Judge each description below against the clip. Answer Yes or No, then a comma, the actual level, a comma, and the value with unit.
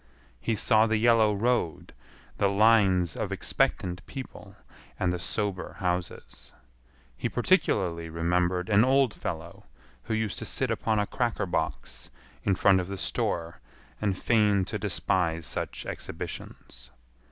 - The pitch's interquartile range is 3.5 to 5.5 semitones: Yes, average, 3.9 semitones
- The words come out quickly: No, slow, 135 wpm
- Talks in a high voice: No, very low, 95 Hz